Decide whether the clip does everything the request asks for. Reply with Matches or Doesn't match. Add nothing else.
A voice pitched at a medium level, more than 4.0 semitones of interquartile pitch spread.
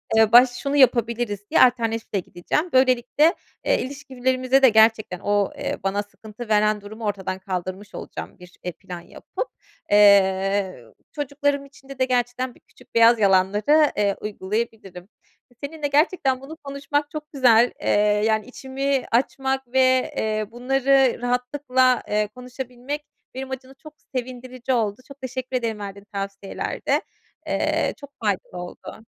Doesn't match